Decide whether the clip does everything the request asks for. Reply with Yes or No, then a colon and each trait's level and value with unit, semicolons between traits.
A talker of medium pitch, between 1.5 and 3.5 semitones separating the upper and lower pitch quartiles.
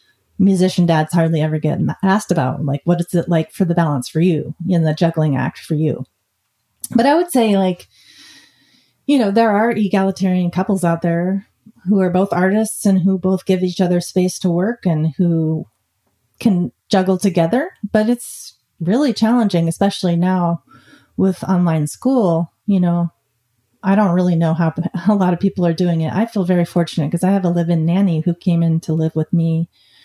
Yes: medium, 175 Hz; average, 3.1 semitones